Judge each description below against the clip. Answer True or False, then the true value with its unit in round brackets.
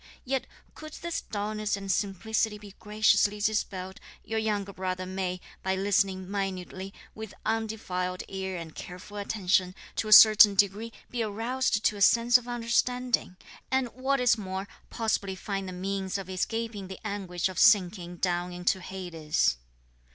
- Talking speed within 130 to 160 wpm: True (150 wpm)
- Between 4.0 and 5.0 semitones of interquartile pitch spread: False (2.9 semitones)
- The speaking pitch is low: False (200 Hz)